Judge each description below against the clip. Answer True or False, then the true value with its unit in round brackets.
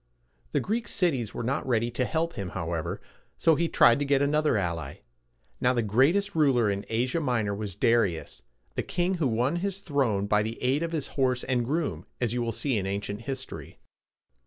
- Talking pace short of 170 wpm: False (200 wpm)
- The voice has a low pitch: True (125 Hz)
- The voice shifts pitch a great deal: True (6.0 semitones)